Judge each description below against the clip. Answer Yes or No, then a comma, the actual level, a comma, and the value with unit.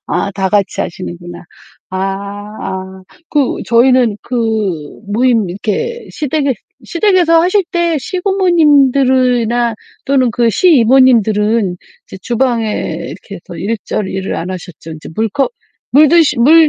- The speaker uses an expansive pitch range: Yes, wide, 6.4 semitones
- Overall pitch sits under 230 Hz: No, high, 240 Hz